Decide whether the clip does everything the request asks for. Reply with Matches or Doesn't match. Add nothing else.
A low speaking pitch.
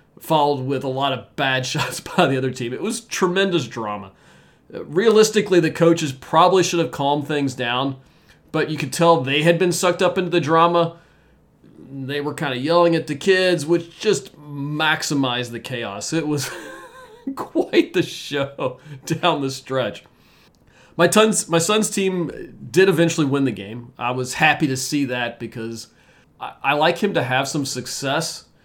Doesn't match